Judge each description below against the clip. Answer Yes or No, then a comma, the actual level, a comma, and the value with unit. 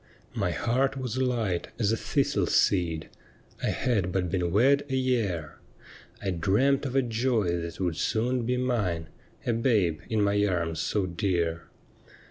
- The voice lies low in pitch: Yes, low, 105 Hz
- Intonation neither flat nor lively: No, wide, 6.2 semitones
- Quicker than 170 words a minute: Yes, average, 180 wpm